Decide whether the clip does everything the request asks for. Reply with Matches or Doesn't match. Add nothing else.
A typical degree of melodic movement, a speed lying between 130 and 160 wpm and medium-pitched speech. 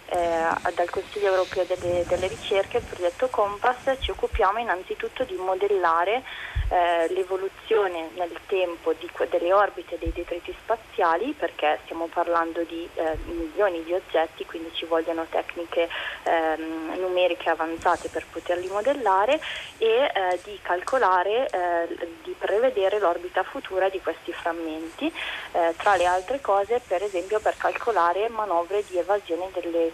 Matches